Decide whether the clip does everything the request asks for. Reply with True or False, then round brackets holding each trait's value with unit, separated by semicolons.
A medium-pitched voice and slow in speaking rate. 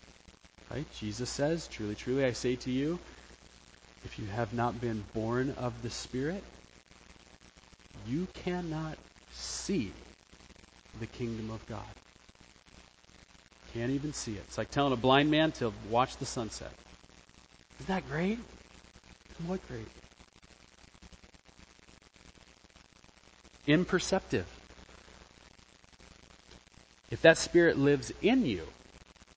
False (110 Hz; 105 wpm)